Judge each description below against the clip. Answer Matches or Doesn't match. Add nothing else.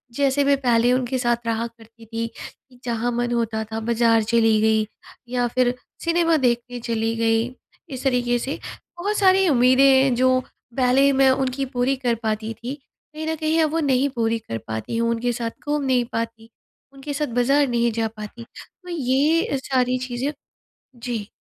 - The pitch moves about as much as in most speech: Matches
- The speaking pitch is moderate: Doesn't match